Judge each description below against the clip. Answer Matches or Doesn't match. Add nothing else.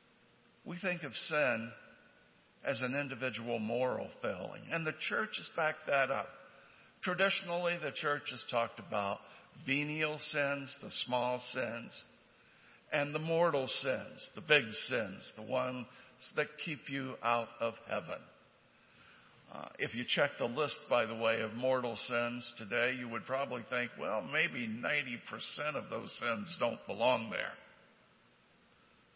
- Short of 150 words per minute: Matches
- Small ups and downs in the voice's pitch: Doesn't match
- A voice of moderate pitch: Doesn't match